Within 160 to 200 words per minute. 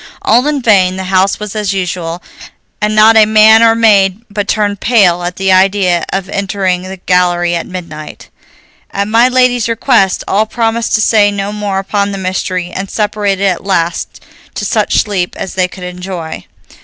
Yes: average, 180 wpm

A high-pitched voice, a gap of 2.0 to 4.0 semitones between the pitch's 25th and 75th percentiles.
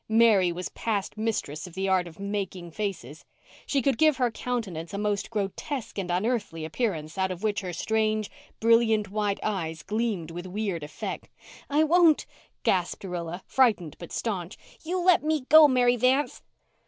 No: high, 205 Hz; average, 5.0 semitones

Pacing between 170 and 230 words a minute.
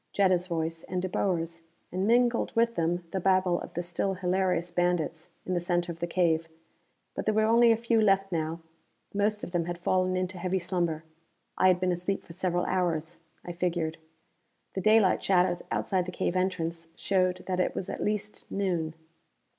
Yes: average, 185 wpm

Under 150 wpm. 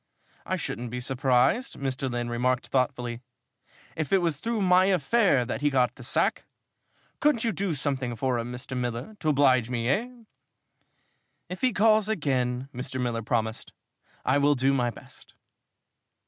No: average, 160 wpm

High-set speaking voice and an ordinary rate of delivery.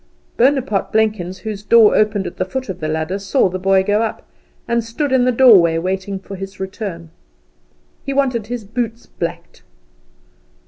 Yes: high, 205 Hz; average, 170 wpm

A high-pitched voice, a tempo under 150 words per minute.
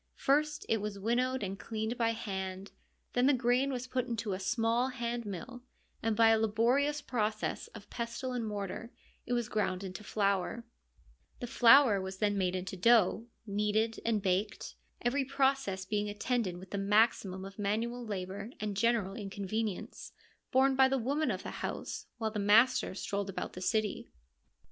No: high, 220 Hz; average, 170 wpm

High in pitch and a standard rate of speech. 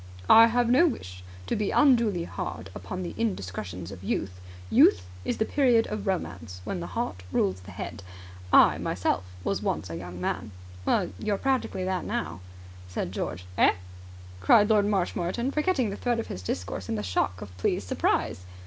No: low, 105 Hz; average, 175 wpm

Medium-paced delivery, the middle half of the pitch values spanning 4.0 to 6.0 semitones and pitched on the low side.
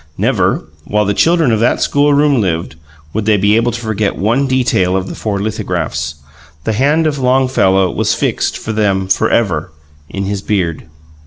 Yes: average, 170 wpm; average, 4.8 semitones; low, 105 Hz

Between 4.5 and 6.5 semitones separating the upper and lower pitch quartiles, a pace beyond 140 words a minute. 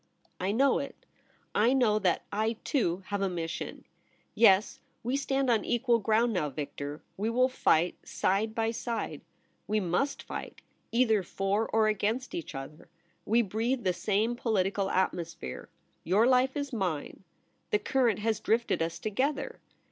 No: average, 4.1 semitones; average, 155 wpm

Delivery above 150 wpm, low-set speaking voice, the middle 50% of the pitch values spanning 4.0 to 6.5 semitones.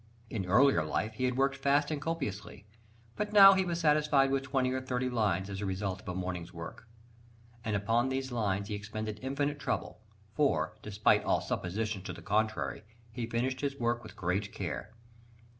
Yes: average, 185 wpm; low, 115 Hz; average, 5.1 semitones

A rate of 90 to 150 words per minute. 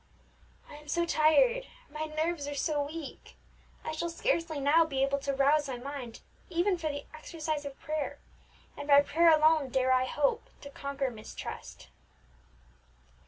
No: average, 160 wpm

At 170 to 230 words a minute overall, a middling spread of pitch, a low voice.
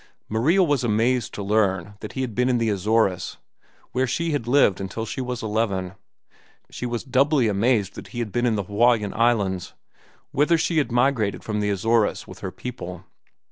Yes: average, 185 wpm; average, 3.5 semitones; low, 115 Hz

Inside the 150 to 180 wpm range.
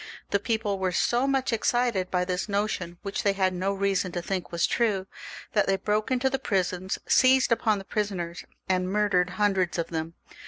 No: average, 190 wpm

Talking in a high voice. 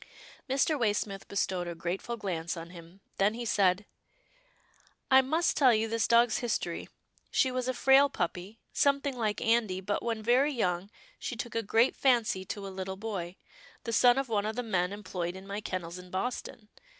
Yes: high, 215 Hz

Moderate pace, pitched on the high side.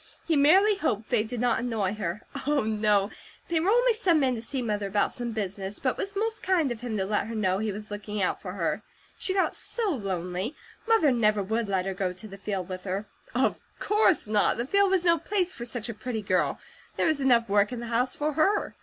No: fast, 240 wpm; high, 230 Hz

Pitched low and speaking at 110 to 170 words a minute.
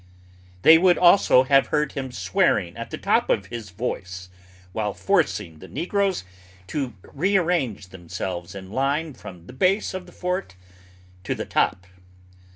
Yes: low, 130 Hz; average, 150 wpm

